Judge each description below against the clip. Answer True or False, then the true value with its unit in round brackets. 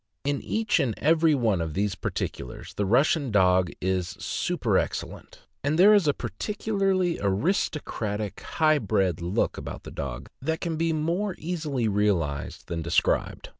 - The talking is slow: False (145 wpm)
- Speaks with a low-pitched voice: True (130 Hz)